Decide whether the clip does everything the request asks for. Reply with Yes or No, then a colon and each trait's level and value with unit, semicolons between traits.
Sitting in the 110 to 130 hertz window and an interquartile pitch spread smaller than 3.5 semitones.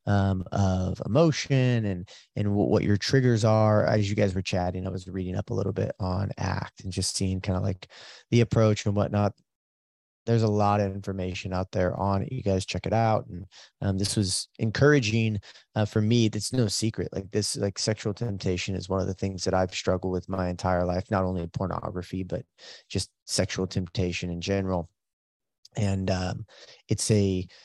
No: very low, 95 Hz; narrow, 2.5 semitones